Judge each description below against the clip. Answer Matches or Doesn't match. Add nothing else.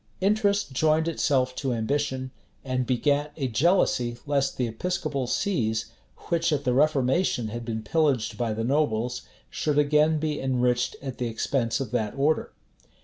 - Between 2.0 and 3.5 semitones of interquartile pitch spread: Doesn't match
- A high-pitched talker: Doesn't match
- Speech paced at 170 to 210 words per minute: Doesn't match